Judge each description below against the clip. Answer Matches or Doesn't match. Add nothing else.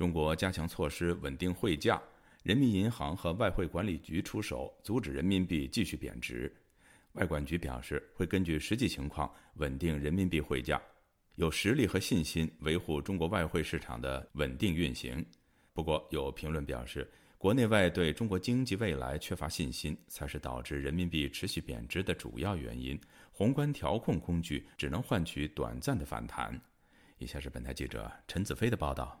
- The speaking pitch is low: Matches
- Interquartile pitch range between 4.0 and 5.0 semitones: Matches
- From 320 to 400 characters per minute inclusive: Doesn't match